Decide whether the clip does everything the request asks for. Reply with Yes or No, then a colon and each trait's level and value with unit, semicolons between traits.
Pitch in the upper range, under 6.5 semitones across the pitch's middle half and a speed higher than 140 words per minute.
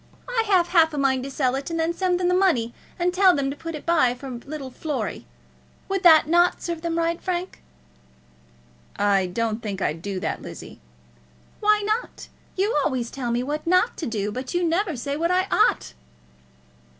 Yes: very high, 320 Hz; wide, 6.0 semitones; average, 200 wpm